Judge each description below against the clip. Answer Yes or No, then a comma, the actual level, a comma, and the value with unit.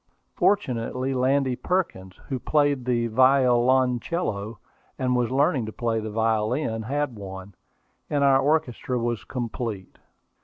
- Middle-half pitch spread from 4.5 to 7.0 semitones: No, average, 3.2 semitones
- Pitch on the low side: Yes, low, 125 Hz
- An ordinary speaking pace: No, slow, 120 wpm